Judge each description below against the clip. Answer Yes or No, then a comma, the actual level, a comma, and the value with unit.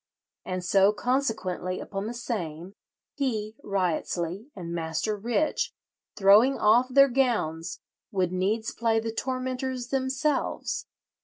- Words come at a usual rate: No, slow, 110 wpm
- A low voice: No, high, 215 Hz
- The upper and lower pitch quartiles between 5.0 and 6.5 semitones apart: Yes, wide, 5.6 semitones